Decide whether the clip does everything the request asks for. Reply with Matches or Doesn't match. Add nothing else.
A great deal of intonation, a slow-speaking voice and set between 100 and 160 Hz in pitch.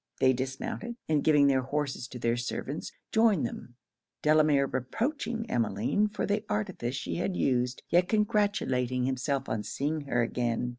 Doesn't match